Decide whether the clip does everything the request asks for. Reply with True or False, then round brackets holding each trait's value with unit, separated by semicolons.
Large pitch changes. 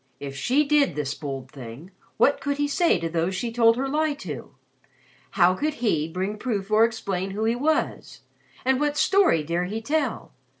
True (9.0 semitones)